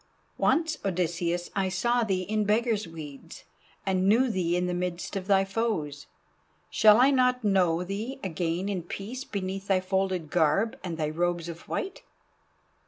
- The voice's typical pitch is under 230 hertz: Yes, high, 190 Hz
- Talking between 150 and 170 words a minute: Yes, average, 160 wpm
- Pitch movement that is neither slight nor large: Yes, average, 3.6 semitones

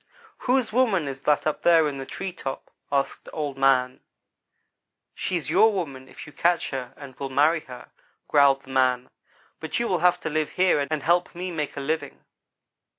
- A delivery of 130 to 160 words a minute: No, average, 190 wpm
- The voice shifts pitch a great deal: No, average, 4.4 semitones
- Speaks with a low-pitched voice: No, medium, 150 Hz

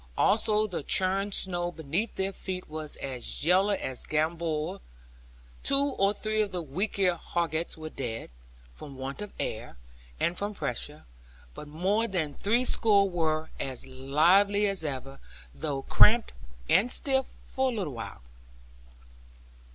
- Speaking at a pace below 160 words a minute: Yes, average, 140 wpm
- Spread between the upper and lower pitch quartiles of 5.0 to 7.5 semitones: Yes, average, 5.3 semitones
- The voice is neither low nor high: Yes, medium, 175 Hz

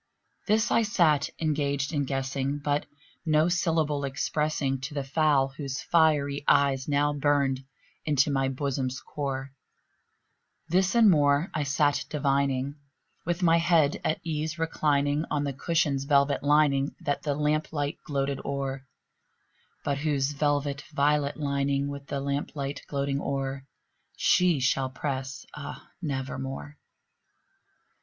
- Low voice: No, medium, 145 Hz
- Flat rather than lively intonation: Yes, narrow, 1.7 semitones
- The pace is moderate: No, slow, 130 wpm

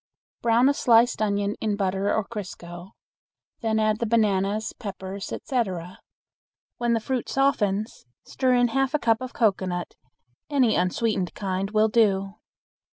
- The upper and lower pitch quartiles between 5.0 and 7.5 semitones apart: No, average, 3.3 semitones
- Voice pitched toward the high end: Yes, high, 215 Hz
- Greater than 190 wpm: No, average, 140 wpm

